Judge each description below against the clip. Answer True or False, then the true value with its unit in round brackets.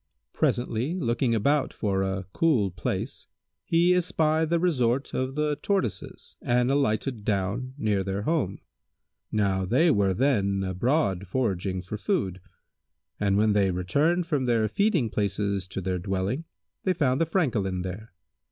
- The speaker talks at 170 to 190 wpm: False (145 wpm)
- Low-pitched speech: True (115 Hz)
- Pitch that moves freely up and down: True (7.2 semitones)